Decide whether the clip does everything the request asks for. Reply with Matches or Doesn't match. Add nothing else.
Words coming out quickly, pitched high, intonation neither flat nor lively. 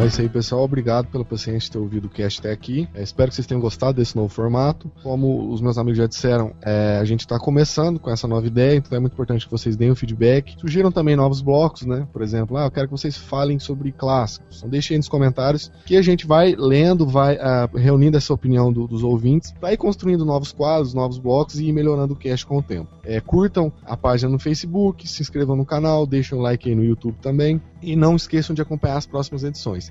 Doesn't match